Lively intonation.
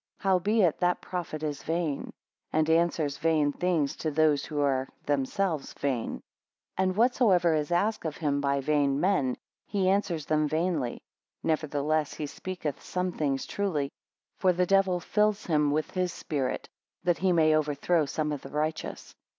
No: average, 3.7 semitones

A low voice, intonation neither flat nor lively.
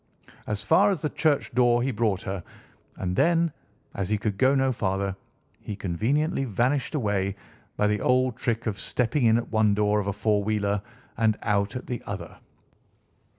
Yes: low, 110 Hz; average, 4.0 semitones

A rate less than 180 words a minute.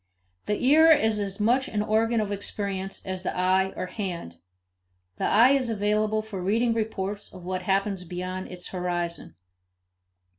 Yes: average, 155 wpm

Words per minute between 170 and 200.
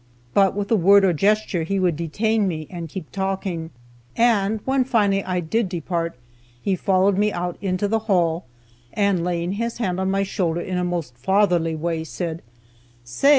Yes: average, 180 wpm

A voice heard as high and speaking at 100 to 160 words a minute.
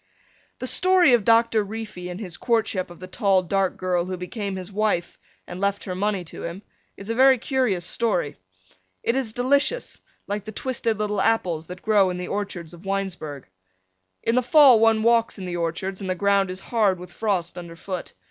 No: high, 200 Hz; average, 195 wpm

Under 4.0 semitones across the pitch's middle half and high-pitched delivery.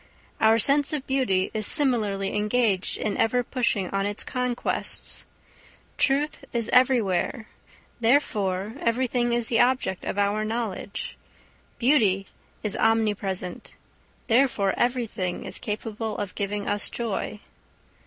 Yes: average, 3.6 semitones; high, 220 Hz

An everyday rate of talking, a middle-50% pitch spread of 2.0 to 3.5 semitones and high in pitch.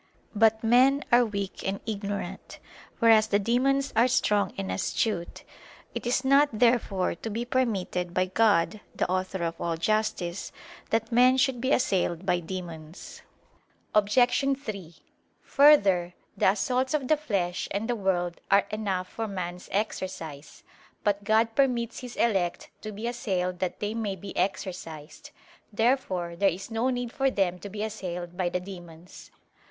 No: average, 155 wpm; average, 4.6 semitones; high, 205 Hz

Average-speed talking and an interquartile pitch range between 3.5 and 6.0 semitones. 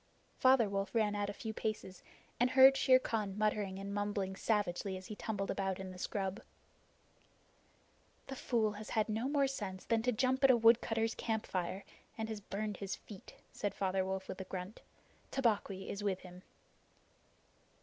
No: average, 170 wpm; average, 2.8 semitones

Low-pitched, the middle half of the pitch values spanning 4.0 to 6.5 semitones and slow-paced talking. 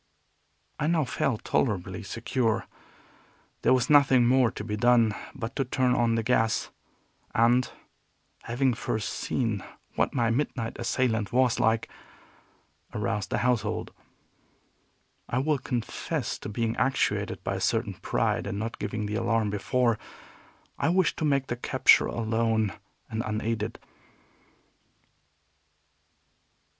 No: low, 115 Hz; average, 2.7 semitones; slow, 125 wpm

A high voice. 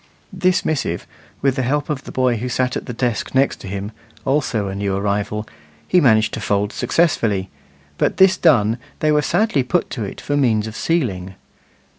No: low, 125 Hz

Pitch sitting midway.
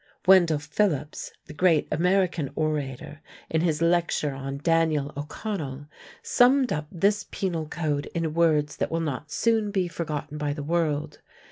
Yes: medium, 160 Hz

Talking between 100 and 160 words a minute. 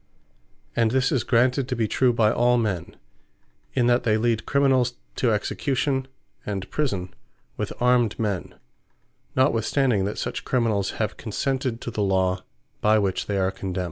Yes: average, 155 wpm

